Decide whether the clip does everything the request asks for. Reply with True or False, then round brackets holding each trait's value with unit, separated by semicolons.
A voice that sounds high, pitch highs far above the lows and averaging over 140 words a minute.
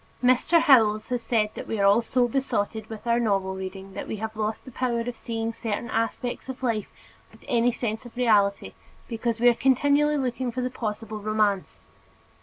False (230 Hz; 2.7 semitones; 195 wpm)